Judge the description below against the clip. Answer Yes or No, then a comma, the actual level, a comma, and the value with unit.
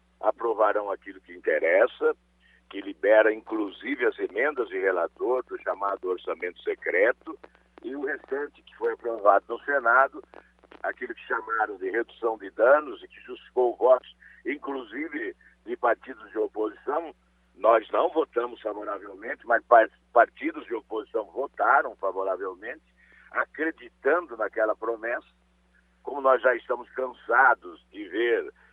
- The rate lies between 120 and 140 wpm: Yes, average, 125 wpm